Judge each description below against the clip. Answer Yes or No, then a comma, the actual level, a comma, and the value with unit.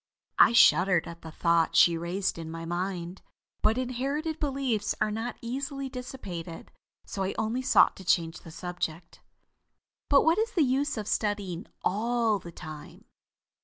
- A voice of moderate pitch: No, high, 205 Hz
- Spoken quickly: No, average, 155 wpm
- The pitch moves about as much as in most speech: No, wide, 7.0 semitones